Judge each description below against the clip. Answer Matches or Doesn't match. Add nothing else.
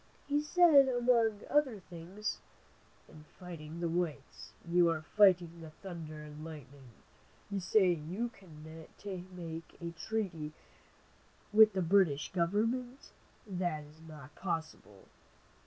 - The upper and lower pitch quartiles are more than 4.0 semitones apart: Matches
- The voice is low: Doesn't match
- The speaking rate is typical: Doesn't match